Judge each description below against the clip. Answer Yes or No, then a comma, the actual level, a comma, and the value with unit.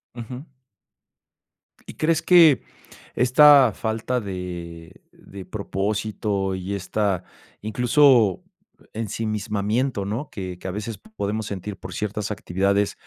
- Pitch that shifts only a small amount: No, average, 3.7 semitones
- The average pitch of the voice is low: Yes, low, 105 Hz